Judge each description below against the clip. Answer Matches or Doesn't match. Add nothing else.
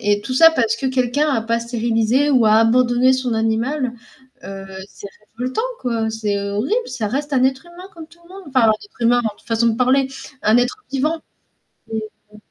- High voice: Matches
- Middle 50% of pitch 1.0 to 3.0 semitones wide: Doesn't match